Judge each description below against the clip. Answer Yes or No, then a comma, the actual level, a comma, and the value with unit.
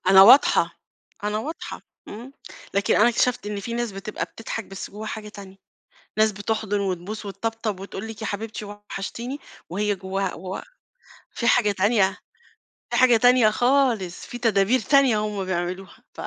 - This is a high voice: Yes, high, 210 Hz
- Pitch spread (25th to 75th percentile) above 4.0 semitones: No, average, 2.9 semitones